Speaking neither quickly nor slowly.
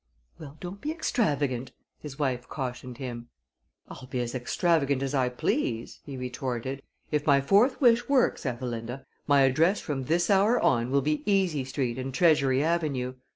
Yes: average, 160 wpm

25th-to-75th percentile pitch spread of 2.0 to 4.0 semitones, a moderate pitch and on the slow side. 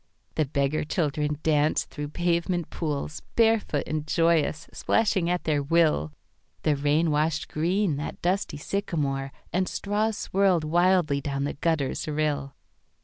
Yes: average, 3.1 semitones; medium, 155 Hz; slow, 120 wpm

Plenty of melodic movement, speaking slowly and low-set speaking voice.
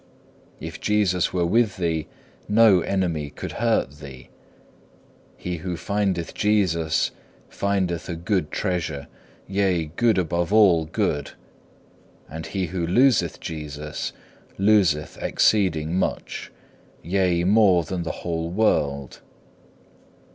No: average, 3.8 semitones; slow, 110 wpm; very low, 90 Hz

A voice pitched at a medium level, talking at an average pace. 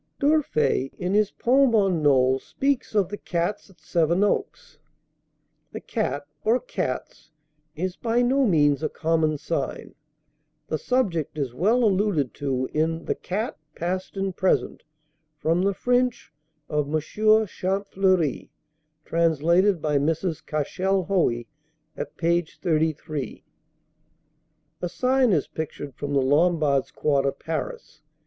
No: medium, 170 Hz; slow, 125 wpm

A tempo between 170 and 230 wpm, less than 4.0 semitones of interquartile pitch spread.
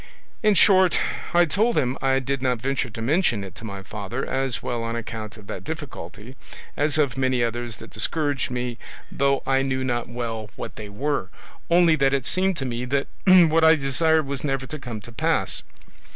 No: average, 195 wpm; average, 4.3 semitones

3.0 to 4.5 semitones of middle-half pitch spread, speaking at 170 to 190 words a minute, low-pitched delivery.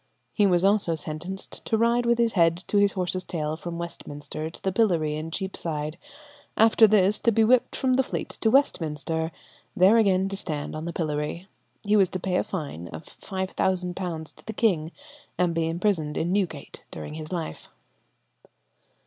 No: average, 4.2 semitones; average, 175 wpm; medium, 180 Hz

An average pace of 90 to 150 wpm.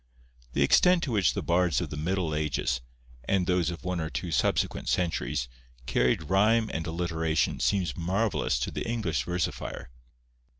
No: average, 160 wpm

